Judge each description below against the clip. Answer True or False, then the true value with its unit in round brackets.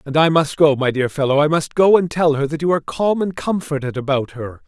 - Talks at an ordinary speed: False (270 wpm)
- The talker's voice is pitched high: False (150 Hz)